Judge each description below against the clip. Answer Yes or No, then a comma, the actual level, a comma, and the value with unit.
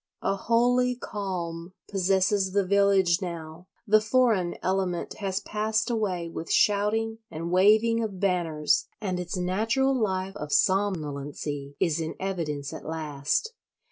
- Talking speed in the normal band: No, slow, 130 wpm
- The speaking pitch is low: No, high, 190 Hz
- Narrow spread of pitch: No, average, 4.1 semitones